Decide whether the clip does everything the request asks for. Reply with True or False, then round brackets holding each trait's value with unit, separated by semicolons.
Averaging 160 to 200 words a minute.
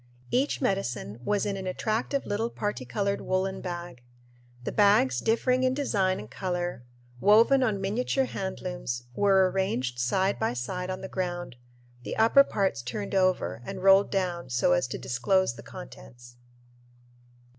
False (150 wpm)